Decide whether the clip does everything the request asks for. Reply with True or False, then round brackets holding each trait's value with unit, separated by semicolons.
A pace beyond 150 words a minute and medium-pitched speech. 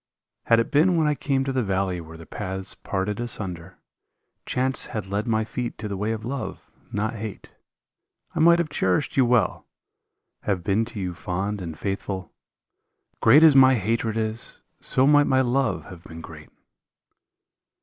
False (170 wpm; 110 Hz)